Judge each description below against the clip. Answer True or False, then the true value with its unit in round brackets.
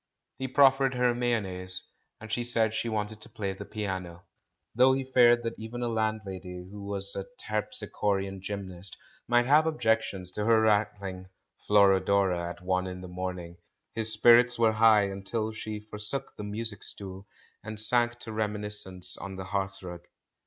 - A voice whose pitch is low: True (105 Hz)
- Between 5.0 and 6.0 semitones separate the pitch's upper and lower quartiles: False (3.3 semitones)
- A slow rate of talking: False (165 wpm)